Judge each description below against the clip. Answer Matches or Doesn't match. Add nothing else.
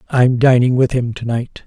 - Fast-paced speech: Matches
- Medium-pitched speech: Doesn't match